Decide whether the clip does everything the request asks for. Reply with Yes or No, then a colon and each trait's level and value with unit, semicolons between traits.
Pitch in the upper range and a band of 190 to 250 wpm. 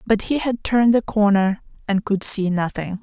Yes: high, 205 Hz; average, 200 wpm